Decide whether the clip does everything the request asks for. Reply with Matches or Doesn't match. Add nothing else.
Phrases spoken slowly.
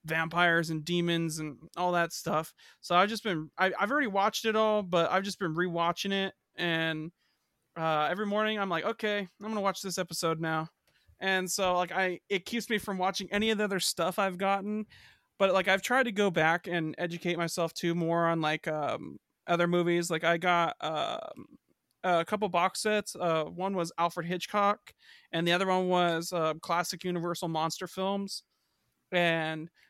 Doesn't match